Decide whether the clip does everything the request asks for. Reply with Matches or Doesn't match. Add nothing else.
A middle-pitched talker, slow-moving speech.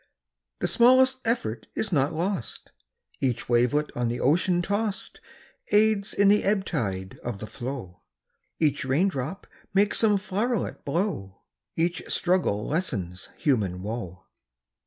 Matches